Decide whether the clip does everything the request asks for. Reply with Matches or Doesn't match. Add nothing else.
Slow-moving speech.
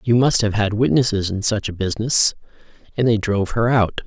Doesn't match